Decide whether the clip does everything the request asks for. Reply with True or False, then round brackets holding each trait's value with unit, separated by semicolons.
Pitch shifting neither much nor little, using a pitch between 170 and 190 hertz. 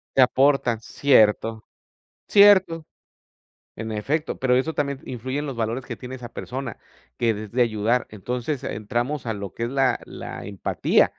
False (3.5 semitones; 125 Hz)